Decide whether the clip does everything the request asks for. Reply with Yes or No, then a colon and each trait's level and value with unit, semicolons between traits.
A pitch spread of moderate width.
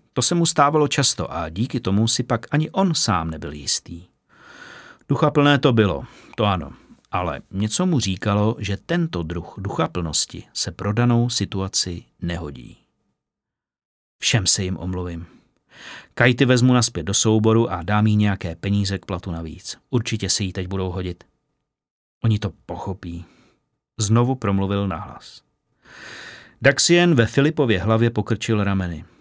Yes: average, 5.0 semitones